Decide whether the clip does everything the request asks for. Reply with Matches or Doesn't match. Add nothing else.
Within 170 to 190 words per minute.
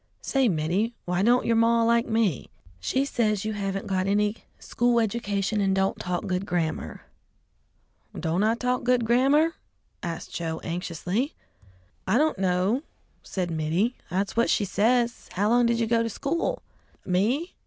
Doesn't match